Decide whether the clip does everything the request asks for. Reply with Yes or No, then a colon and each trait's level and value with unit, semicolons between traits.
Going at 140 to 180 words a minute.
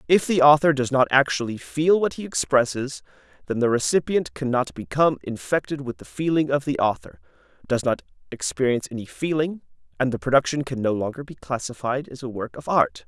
No: average, 190 wpm